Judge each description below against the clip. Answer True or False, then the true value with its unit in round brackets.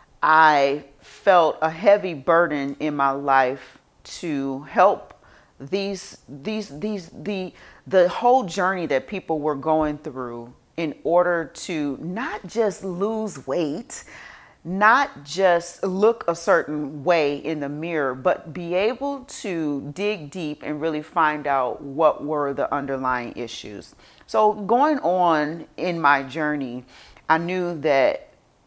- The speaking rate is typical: False (130 wpm)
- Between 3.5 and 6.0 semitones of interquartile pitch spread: True (4.7 semitones)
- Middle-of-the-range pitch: True (160 Hz)